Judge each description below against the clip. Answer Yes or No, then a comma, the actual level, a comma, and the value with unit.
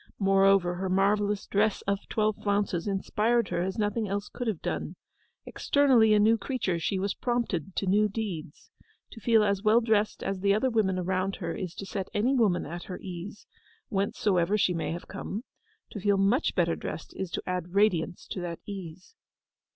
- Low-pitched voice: No, high, 200 Hz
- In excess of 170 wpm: Yes, average, 185 wpm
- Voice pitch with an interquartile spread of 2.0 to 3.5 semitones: Yes, narrow, 2.5 semitones